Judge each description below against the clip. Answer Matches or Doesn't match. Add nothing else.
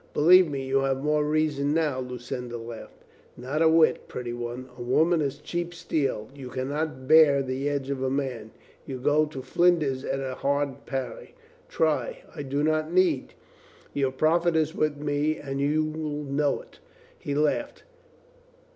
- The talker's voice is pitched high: Doesn't match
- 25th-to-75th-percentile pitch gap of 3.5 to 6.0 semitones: Doesn't match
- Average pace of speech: Matches